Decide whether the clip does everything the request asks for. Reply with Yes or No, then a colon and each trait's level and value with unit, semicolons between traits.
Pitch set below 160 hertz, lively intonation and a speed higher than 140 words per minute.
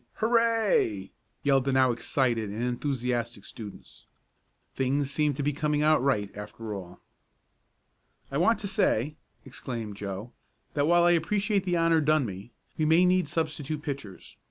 Yes: medium, 140 Hz; wide, 5.8 semitones; average, 150 wpm